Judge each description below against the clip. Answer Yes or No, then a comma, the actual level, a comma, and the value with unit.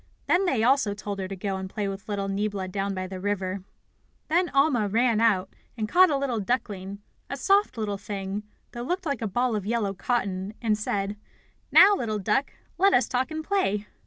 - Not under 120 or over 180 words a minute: No, average, 200 wpm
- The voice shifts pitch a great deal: No, average, 4.6 semitones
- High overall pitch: Yes, high, 210 Hz